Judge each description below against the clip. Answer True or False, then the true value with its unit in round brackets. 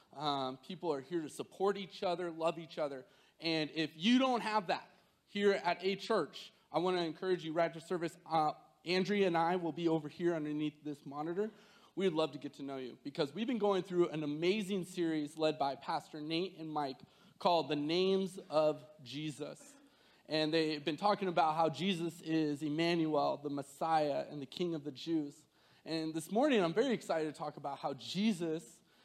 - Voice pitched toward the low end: False (165 Hz)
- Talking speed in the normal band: True (195 wpm)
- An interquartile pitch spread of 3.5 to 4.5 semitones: True (3.8 semitones)